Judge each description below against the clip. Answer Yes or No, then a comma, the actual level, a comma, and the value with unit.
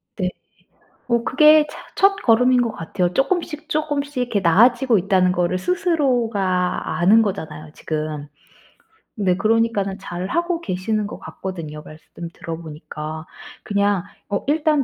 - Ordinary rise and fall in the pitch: No, wide, 6.9 semitones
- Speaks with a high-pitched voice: Yes, high, 205 Hz